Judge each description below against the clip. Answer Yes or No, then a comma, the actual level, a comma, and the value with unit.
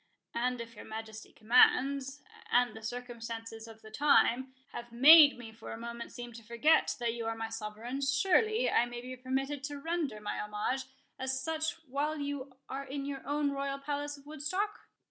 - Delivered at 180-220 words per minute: Yes, average, 185 wpm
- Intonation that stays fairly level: No, average, 3.6 semitones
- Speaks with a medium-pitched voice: No, very high, 260 Hz